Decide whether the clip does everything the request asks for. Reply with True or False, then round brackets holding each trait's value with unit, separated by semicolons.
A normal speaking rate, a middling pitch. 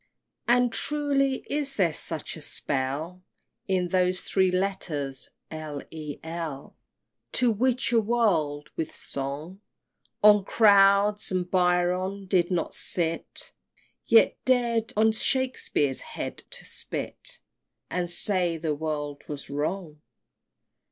False (120 wpm; 180 Hz)